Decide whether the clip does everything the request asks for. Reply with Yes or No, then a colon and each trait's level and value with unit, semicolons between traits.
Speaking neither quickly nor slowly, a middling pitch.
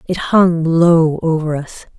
Yes: average, 150 wpm; medium, 165 Hz